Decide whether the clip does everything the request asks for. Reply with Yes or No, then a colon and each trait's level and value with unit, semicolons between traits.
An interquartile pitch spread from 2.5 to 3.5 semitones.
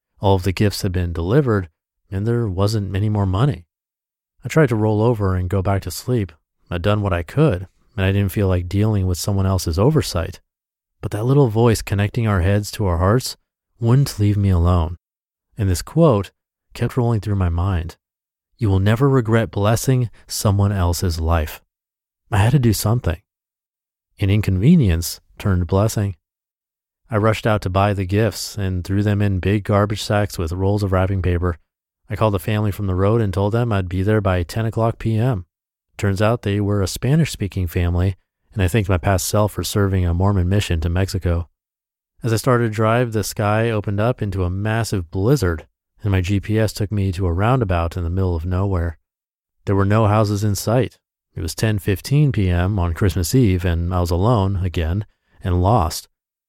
Yes: average, 3.2 semitones